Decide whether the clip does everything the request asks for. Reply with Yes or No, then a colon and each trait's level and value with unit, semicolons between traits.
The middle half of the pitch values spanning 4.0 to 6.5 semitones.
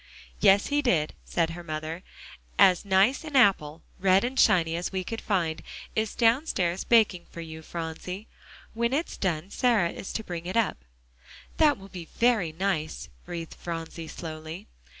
Yes: average, 5.1 semitones